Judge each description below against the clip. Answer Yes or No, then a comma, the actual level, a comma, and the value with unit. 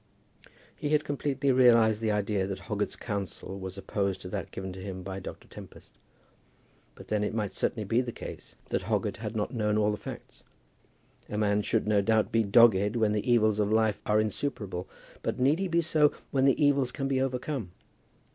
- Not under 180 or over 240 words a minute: Yes, average, 195 wpm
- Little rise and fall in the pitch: No, average, 4.1 semitones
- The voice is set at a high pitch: No, low, 110 Hz